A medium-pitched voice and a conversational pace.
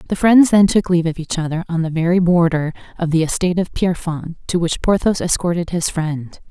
No: medium, 170 Hz; fast, 210 wpm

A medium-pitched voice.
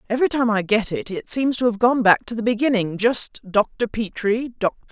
No: high, 225 Hz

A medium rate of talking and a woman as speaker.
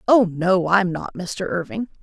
Yes: average, 180 wpm; female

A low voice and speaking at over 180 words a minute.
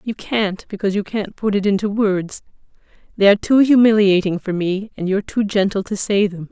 No: high, 200 Hz; average, 195 wpm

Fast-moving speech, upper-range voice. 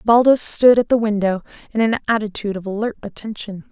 No: average, 180 wpm; high, 215 Hz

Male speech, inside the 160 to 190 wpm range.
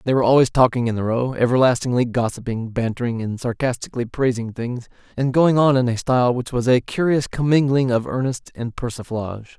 Yes: male; average, 180 wpm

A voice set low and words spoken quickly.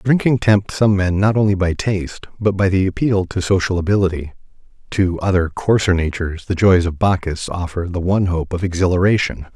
No: very low, 95 Hz; average, 175 wpm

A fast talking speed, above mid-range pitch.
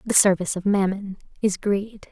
No: average, 170 wpm; high, 200 Hz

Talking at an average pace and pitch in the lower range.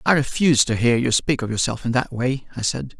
No: fast, 260 wpm; low, 125 Hz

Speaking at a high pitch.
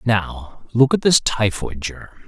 No: low, 110 Hz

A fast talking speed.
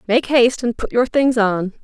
Yes: fast, 230 wpm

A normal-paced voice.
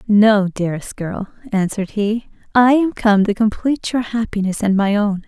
Yes: average, 170 wpm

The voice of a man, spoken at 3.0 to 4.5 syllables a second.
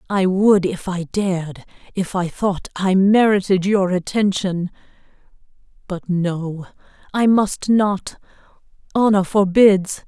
No: female; 3.7 syllables/s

